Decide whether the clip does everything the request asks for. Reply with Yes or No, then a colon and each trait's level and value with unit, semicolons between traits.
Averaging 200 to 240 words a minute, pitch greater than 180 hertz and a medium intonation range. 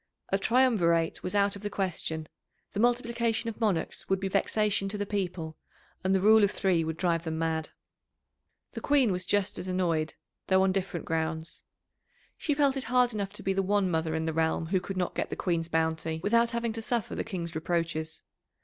Yes: fast, 205 wpm; high, 190 Hz; average, 4.5 semitones